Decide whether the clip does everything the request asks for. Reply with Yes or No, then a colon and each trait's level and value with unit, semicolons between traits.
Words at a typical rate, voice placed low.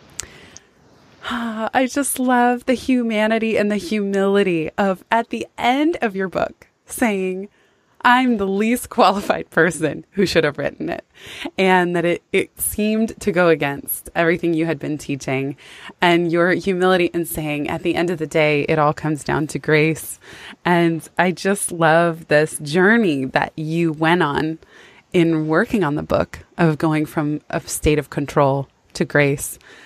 No: average, 160 wpm; medium, 170 Hz